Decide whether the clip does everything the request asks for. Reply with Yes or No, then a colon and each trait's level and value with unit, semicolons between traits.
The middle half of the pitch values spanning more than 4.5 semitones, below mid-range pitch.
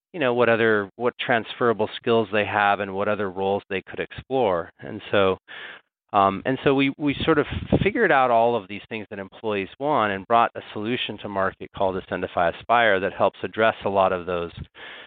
No: average, 3.3 semitones; low, 105 Hz